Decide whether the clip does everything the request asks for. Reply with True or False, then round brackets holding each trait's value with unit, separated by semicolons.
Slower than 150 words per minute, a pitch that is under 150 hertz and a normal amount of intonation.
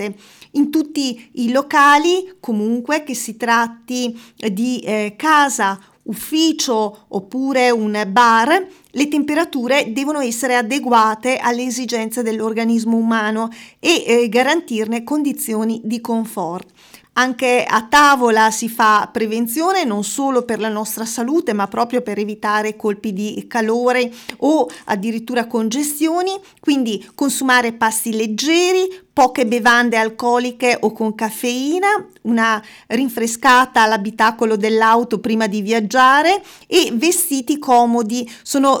False (115 wpm; 240 Hz; 3.7 semitones)